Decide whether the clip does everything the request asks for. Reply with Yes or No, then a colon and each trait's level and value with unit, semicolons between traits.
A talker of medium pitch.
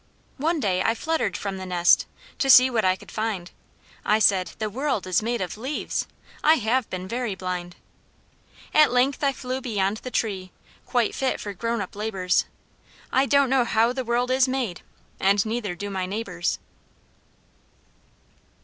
No: high, 220 Hz